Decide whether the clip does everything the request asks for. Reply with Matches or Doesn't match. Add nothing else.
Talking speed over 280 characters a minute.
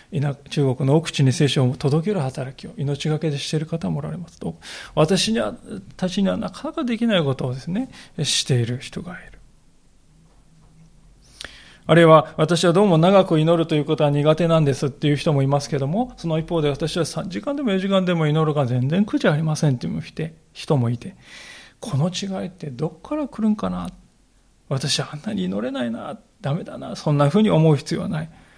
Matches